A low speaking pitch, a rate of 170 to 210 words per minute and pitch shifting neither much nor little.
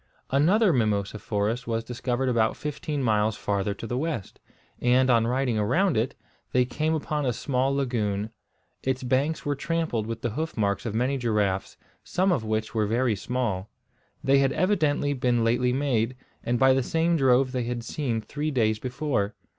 Yes: low, 125 Hz; average, 175 wpm; average, 3.9 semitones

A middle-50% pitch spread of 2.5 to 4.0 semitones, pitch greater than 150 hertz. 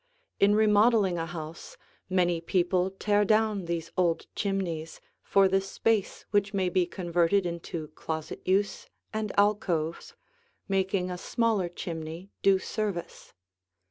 Yes: average, 3.0 semitones; medium, 185 Hz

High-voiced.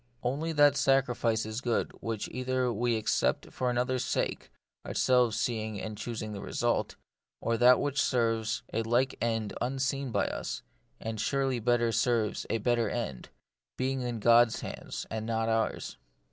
No: low, 120 Hz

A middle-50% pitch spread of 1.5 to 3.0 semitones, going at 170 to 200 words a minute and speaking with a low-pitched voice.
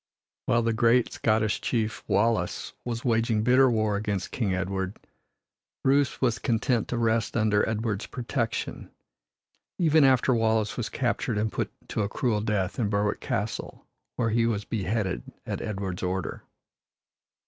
No: narrow, 2.4 semitones; average, 145 wpm; low, 110 Hz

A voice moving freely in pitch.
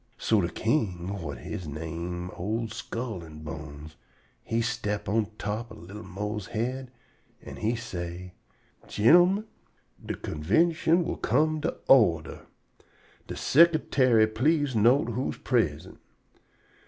Yes: wide, 6.4 semitones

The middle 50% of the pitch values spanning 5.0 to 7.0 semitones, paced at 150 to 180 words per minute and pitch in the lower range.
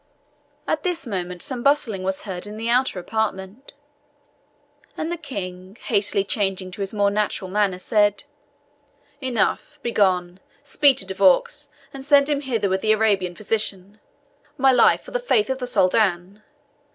No: wide, 5.5 semitones; average, 155 wpm; high, 210 Hz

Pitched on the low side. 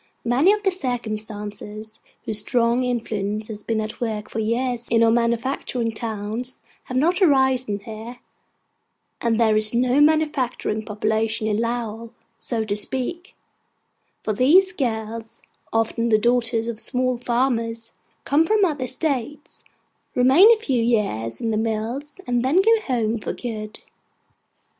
No: high, 235 Hz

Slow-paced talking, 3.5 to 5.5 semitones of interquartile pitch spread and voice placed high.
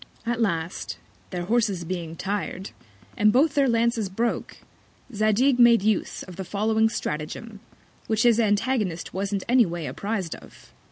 No: average, 145 wpm; average, 3.9 semitones; high, 210 Hz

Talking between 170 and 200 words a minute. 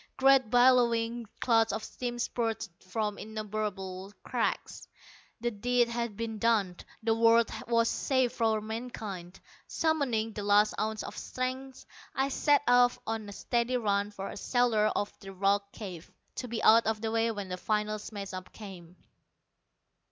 No: average, 155 wpm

